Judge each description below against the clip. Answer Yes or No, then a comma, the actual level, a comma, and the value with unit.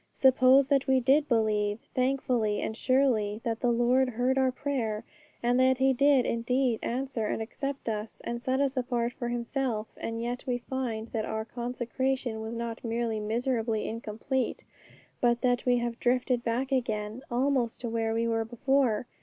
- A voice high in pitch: Yes, high, 240 Hz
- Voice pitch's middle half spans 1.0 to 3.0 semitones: Yes, narrow, 2.4 semitones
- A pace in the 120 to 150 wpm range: No, average, 170 wpm